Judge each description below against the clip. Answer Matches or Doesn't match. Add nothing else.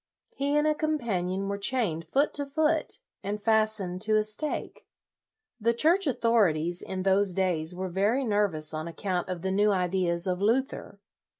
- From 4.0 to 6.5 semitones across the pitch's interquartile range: Matches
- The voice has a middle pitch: Doesn't match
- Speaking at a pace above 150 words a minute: Matches